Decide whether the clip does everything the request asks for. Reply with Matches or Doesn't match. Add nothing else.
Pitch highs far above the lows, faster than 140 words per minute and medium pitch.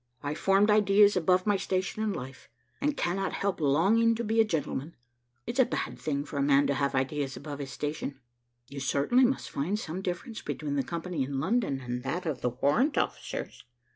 Matches